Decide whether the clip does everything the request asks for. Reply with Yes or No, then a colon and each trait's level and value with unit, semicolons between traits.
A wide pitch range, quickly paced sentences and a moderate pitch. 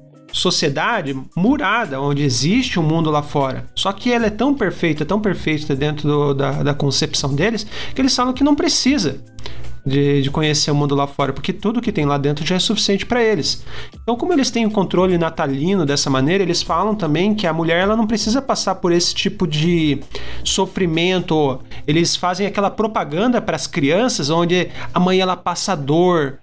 Yes: wide, 5.7 semitones; fast, 195 wpm; medium, 170 Hz